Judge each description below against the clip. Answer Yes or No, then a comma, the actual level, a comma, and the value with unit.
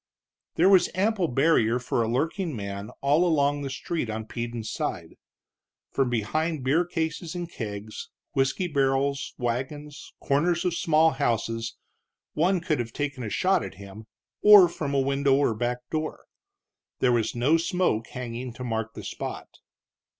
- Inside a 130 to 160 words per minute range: Yes, average, 155 wpm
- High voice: No, medium, 140 Hz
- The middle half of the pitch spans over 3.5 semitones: Yes, wide, 5.4 semitones